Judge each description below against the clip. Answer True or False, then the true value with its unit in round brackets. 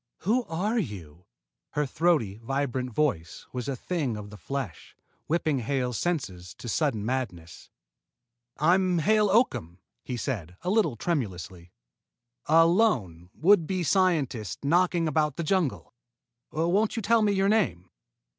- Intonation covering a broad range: True (8.8 semitones)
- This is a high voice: False (145 Hz)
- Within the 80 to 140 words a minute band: True (135 wpm)